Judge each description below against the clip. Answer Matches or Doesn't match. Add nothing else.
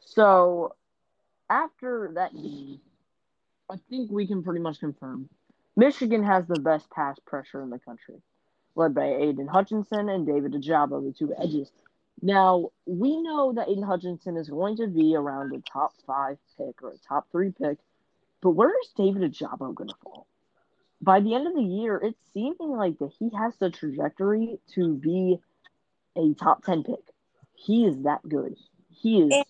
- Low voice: Doesn't match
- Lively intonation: Matches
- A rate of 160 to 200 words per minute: Matches